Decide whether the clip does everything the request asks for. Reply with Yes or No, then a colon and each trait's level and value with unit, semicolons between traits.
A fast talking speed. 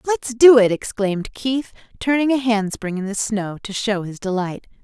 No: average, 185 wpm